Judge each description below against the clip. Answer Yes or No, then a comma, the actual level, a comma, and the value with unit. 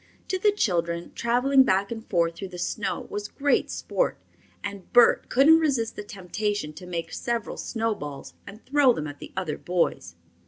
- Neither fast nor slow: Yes, average, 170 wpm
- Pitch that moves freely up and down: Yes, wide, 5.8 semitones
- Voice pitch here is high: Yes, high, 205 Hz